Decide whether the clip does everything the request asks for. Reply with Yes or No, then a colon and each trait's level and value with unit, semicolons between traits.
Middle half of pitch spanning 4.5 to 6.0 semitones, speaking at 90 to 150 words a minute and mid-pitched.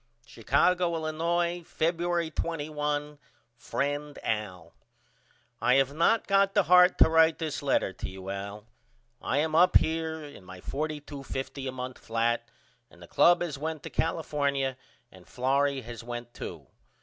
Yes: average, 5.2 semitones; average, 145 wpm; medium, 145 Hz